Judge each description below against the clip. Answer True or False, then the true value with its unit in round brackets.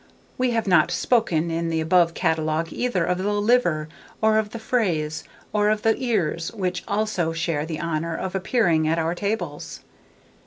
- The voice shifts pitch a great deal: False (4.7 semitones)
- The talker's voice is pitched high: False (180 Hz)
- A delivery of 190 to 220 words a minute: False (170 wpm)